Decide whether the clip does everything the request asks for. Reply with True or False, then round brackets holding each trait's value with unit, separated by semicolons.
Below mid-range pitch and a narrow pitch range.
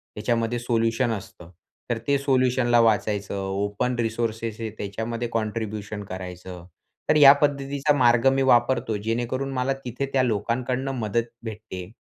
False (115 Hz; 3.2 semitones)